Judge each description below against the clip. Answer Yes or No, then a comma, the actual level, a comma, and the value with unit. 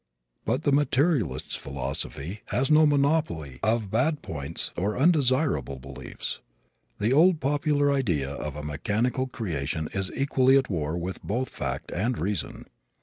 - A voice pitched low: Yes, low, 115 Hz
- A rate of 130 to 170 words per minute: Yes, average, 140 wpm